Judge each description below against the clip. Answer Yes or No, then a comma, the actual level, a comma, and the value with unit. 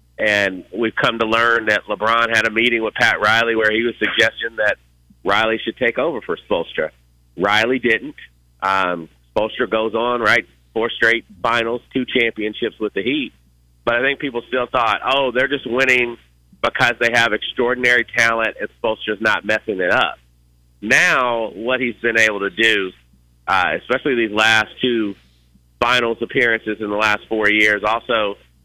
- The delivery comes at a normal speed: Yes, average, 170 wpm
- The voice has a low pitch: Yes, low, 110 Hz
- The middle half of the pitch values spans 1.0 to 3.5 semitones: No, average, 4.2 semitones